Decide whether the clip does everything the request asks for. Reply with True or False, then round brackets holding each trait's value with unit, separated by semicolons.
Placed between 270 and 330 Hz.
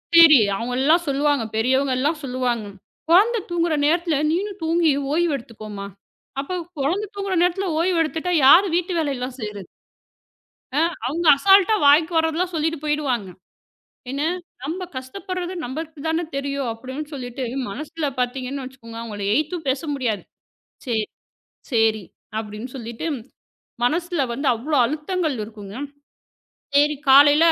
True (290 Hz)